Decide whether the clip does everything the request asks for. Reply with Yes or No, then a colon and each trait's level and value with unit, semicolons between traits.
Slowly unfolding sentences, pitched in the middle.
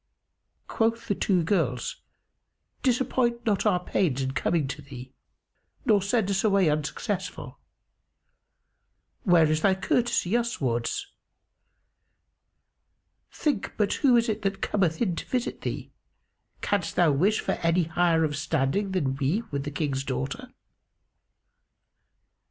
Yes: slow, 125 wpm; medium, 180 Hz